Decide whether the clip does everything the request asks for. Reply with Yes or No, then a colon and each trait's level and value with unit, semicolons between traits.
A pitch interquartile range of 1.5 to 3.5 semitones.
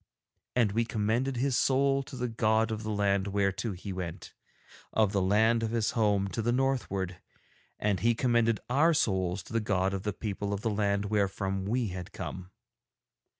Yes: average, 3.1 semitones